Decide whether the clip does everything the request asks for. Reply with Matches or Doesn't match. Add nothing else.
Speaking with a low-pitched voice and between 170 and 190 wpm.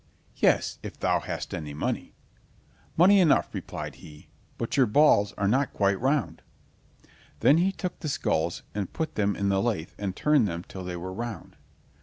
Matches